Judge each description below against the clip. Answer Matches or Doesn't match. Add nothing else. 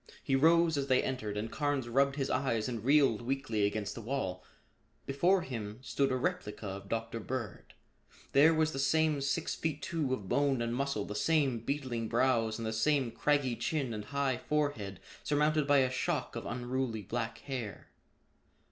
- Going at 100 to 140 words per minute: Doesn't match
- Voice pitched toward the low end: Matches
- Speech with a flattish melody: Doesn't match